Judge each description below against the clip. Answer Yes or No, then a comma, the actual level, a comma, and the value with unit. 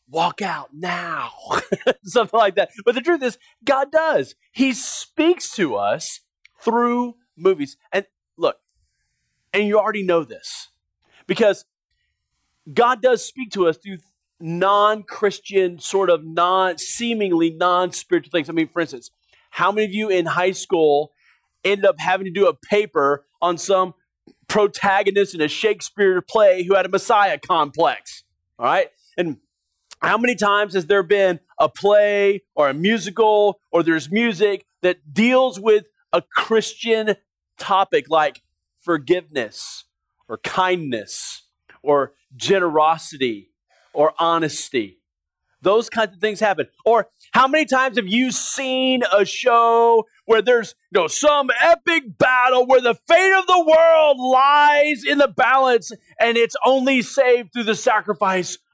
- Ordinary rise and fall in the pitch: No, wide, 5.7 semitones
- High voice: Yes, high, 210 Hz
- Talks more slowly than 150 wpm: Yes, average, 140 wpm